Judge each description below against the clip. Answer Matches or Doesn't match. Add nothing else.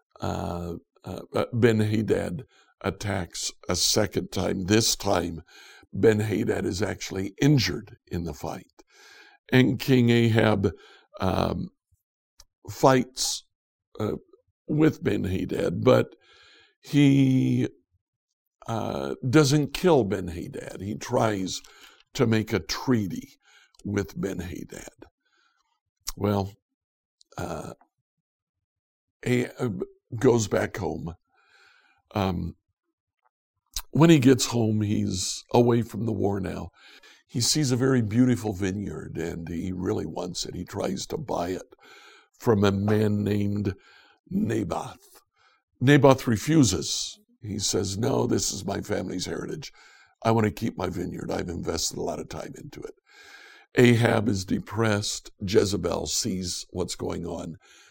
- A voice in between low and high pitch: Doesn't match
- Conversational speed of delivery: Doesn't match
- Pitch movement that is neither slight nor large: Matches